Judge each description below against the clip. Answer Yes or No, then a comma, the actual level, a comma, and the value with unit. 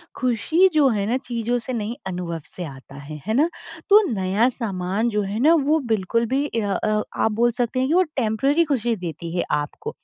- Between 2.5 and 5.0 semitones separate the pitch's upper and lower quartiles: No, wide, 5.5 semitones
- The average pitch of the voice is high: Yes, high, 225 Hz